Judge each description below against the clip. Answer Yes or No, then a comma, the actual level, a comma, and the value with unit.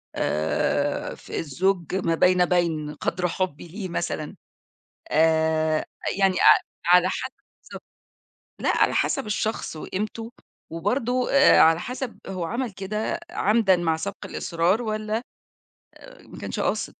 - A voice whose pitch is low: No, medium, 185 Hz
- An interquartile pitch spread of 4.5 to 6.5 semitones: Yes, average, 4.8 semitones